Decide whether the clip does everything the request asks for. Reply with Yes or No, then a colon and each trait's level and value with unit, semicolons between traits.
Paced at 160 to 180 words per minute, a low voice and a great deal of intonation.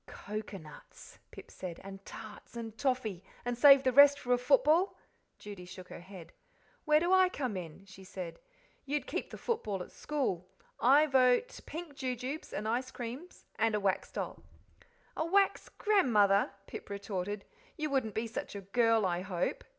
No: average, 165 wpm; high, 230 Hz; wide, 6.4 semitones